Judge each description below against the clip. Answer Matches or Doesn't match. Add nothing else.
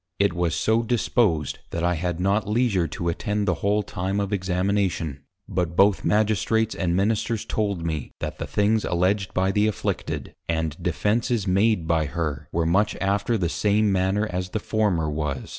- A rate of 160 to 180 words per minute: Matches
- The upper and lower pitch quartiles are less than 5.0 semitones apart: Matches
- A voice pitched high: Doesn't match